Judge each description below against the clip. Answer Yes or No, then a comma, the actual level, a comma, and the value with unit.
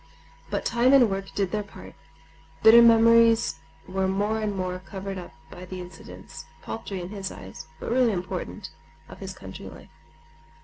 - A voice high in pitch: Yes, high, 195 Hz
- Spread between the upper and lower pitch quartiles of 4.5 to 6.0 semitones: No, average, 3.5 semitones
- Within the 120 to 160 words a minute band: Yes, average, 150 wpm